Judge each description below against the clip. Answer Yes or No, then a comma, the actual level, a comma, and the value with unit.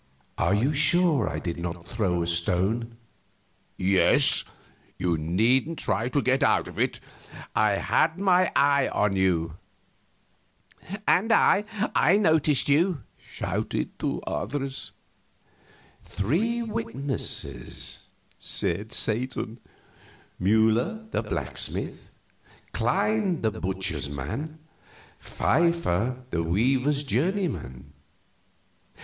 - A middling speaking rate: No, slow, 95 wpm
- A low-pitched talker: Yes, low, 120 Hz